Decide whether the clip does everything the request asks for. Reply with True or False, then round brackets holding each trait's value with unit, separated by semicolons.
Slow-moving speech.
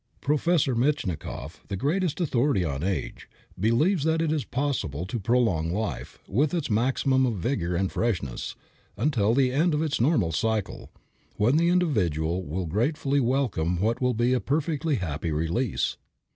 False (155 wpm)